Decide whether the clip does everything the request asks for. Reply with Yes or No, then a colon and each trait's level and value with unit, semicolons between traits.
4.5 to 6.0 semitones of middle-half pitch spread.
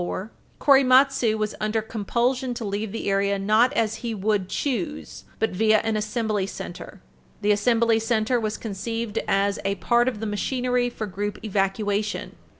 No: average, 2.7 semitones